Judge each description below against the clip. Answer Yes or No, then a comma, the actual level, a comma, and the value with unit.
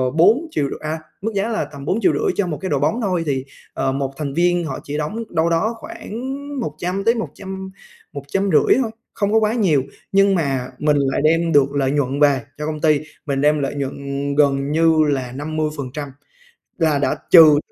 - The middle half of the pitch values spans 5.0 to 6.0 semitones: Yes, average, 5.3 semitones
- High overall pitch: No, medium, 155 Hz